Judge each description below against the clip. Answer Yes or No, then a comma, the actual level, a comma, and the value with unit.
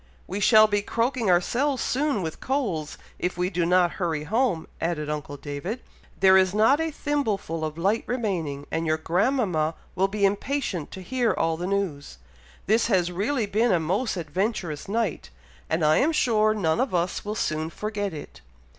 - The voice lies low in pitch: No, high, 190 Hz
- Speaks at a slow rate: No, average, 175 wpm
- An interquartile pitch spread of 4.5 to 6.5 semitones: Yes, wide, 5.5 semitones